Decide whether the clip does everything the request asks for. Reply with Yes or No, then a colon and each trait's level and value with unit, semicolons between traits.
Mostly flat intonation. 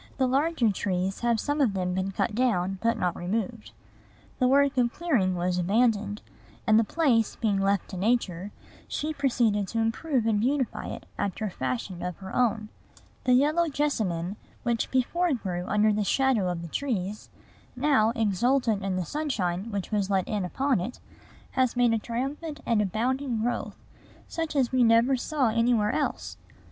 No: average, 5.0 semitones